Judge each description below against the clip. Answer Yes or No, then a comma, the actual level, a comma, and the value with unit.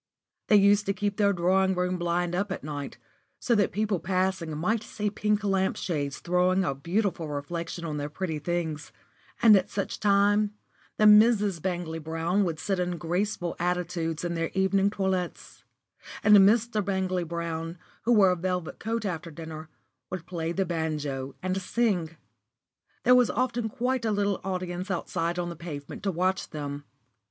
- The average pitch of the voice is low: No, medium, 180 Hz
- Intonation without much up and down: No, average, 3.4 semitones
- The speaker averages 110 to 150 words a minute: No, average, 165 wpm